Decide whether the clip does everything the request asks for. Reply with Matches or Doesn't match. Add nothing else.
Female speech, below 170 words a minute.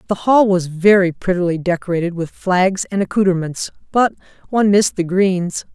Matches